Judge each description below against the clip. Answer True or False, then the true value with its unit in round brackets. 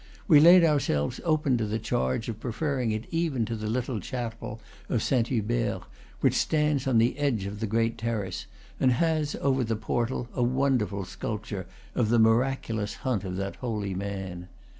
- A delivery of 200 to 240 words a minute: False (180 wpm)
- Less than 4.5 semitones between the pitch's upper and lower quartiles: True (3.8 semitones)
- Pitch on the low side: True (115 Hz)